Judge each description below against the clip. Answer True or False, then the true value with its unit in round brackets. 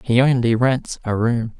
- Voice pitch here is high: False (120 Hz)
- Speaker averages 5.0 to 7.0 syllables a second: False (4.2 syllables/s)